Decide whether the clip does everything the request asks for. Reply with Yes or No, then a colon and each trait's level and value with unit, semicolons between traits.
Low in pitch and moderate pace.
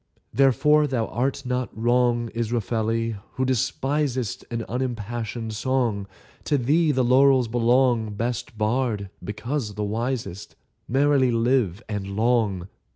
No: low, 120 Hz; slow, 115 wpm